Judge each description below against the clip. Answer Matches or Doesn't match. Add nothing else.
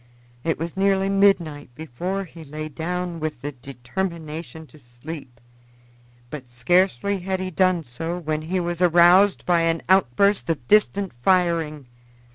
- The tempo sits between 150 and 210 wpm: Doesn't match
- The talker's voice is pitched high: Doesn't match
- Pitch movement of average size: Matches